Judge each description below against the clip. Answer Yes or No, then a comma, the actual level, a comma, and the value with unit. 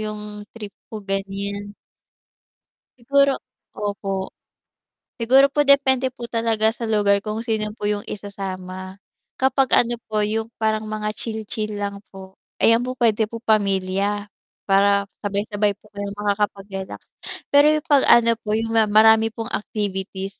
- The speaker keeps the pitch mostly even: Yes, narrow, 2.2 semitones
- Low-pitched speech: No, high, 210 Hz